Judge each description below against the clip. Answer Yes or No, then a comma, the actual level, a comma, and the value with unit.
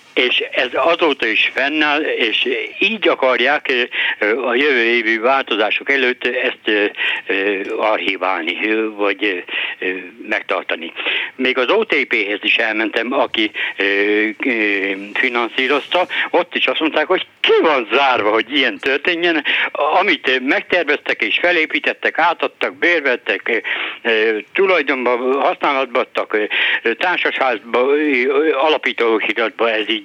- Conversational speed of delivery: No, slow, 95 wpm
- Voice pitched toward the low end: No, medium, 170 Hz